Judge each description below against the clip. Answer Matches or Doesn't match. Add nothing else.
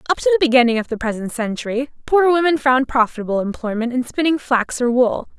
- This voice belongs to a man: Doesn't match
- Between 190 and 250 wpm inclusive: Matches